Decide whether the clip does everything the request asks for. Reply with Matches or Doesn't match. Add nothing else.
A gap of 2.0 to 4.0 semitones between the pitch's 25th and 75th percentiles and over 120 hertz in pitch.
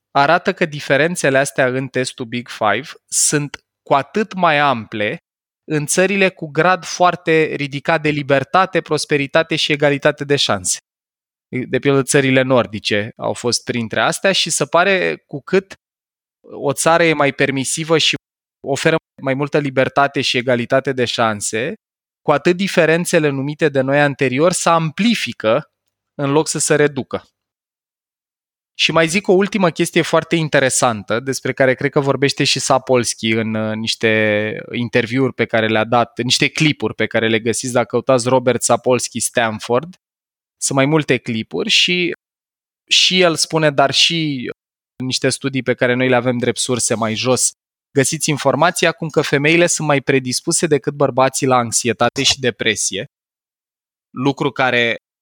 Doesn't match